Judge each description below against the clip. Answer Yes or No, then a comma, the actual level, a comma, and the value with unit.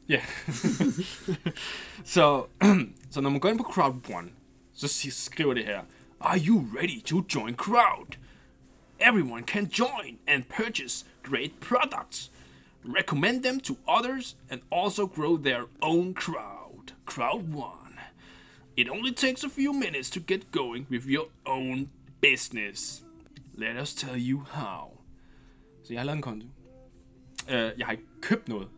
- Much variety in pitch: Yes, wide, 8.0 semitones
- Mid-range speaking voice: Yes, medium, 145 Hz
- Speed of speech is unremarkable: No, slow, 135 wpm